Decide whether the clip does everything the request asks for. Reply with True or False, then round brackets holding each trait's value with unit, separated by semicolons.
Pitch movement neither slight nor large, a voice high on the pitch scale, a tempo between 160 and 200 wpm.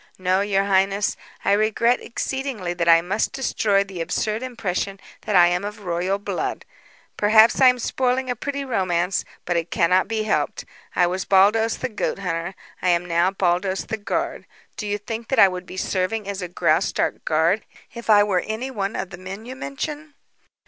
True (3.5 semitones; 200 Hz; 190 wpm)